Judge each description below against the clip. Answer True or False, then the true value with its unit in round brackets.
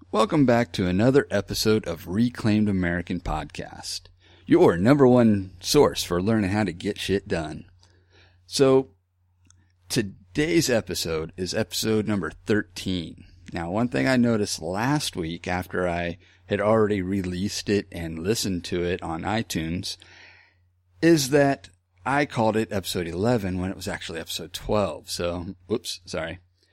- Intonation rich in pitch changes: False (3.4 semitones)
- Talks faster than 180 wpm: False (140 wpm)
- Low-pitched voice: True (95 Hz)